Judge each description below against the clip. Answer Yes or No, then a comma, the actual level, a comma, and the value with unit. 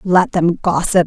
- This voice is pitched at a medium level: Yes, medium, 180 Hz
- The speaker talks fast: No, average, 170 wpm